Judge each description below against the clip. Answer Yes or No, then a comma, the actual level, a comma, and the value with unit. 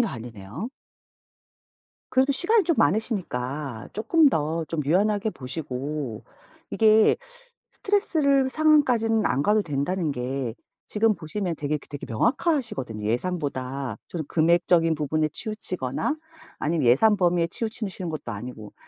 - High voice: No, medium, 170 Hz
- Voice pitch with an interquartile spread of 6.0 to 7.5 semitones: No, wide, 8.3 semitones